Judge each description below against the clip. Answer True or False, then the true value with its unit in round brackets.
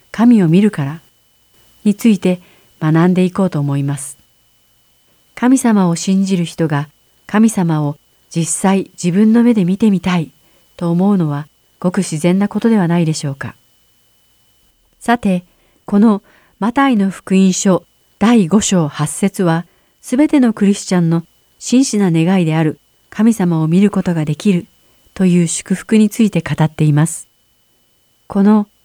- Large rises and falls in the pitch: False (4.1 semitones)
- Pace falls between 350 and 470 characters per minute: False (260 characters per minute)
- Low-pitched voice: False (185 Hz)